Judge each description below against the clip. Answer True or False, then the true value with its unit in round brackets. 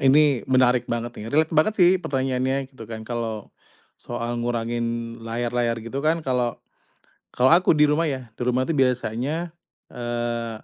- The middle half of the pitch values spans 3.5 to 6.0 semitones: False (2.7 semitones)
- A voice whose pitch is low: True (125 Hz)